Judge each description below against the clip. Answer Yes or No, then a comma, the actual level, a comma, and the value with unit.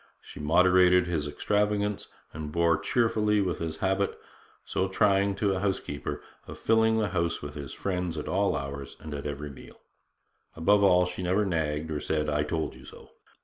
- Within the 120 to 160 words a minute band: No, average, 180 wpm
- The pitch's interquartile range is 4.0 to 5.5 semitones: Yes, average, 4.7 semitones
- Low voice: Yes, very low, 90 Hz